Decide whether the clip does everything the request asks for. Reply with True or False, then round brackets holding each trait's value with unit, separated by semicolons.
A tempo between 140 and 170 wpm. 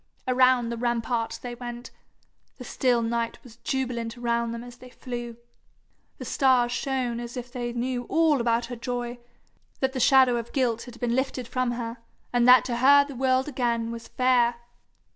False (180 wpm)